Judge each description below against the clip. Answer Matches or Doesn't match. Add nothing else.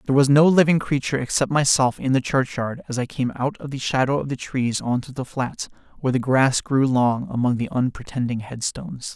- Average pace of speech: Doesn't match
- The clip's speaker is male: Matches